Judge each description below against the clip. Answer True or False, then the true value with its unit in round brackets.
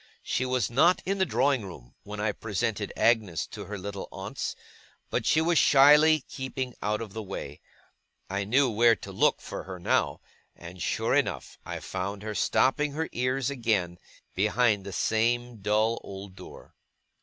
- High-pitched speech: False (110 Hz)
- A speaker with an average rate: True (165 wpm)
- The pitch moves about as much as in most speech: True (4.7 semitones)